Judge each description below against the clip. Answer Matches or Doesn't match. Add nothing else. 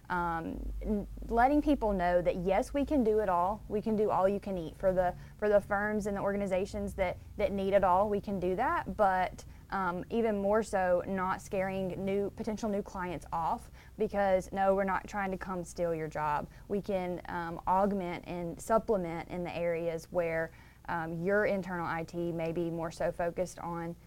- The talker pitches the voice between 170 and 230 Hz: Matches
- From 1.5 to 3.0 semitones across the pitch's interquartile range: Matches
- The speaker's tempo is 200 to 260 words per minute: Doesn't match